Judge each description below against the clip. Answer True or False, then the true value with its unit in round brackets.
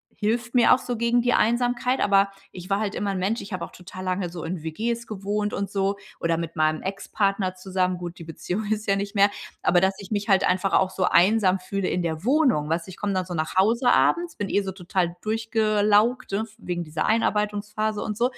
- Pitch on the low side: False (200 Hz)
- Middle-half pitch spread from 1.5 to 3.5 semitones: True (2.9 semitones)